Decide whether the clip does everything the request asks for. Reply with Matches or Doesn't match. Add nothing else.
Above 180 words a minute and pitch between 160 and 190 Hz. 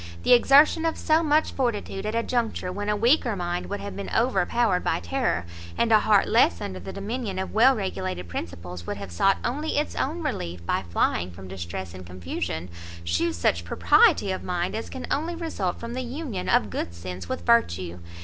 Matches